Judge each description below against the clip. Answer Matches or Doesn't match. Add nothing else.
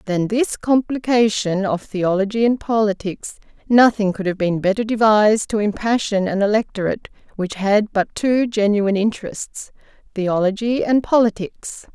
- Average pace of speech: Doesn't match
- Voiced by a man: Doesn't match